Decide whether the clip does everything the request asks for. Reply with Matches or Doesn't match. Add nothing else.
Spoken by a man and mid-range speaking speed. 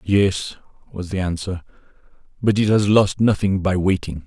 Matches